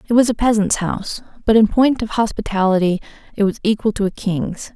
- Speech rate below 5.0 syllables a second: No, 5.8 syllables/s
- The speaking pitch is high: Yes, high, 210 Hz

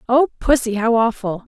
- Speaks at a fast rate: No, average, 155 wpm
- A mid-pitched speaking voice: No, high, 235 Hz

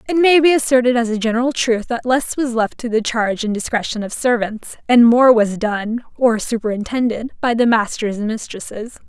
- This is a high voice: Yes, high, 235 Hz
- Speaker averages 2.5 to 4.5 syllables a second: No, 5.3 syllables/s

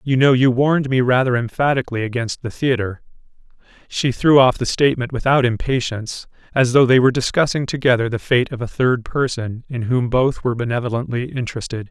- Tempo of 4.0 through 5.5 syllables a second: No, 5.9 syllables/s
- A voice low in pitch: Yes, low, 125 Hz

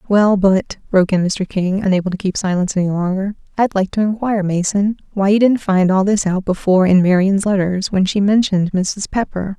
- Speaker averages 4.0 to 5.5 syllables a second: No, 5.7 syllables/s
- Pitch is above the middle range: Yes, high, 195 Hz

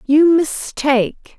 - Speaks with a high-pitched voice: Yes, very high, 290 Hz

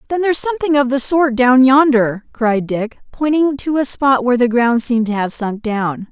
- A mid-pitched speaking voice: No, very high, 255 Hz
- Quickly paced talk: Yes, fast, 215 wpm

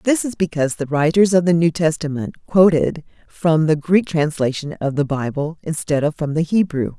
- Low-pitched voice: No, medium, 160 Hz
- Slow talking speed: No, average, 190 wpm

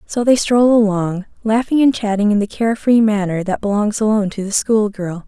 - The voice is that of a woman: Yes, female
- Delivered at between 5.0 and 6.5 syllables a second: Yes, 5.4 syllables/s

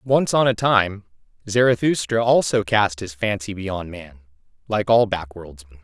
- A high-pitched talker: No, low, 105 Hz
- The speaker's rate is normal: Yes, average, 145 wpm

